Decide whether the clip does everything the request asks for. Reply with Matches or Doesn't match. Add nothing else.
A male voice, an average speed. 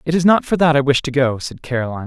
Doesn't match